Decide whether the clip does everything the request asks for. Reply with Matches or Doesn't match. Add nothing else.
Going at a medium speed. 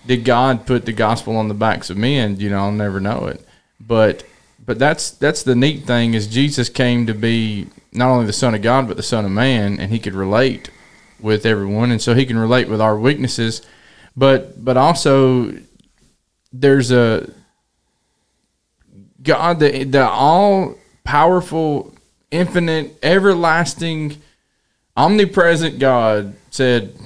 Matches